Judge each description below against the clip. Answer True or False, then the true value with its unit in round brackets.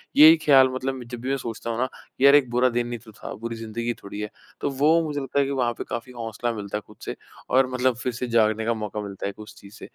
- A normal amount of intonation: True (3.0 semitones)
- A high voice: False (120 Hz)